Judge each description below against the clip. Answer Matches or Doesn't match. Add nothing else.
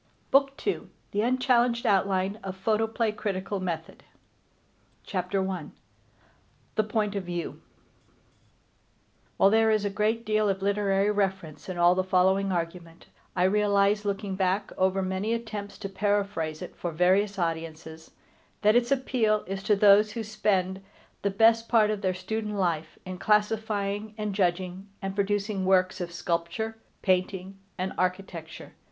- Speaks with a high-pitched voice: Matches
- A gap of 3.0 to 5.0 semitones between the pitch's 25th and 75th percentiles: Doesn't match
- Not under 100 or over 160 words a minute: Matches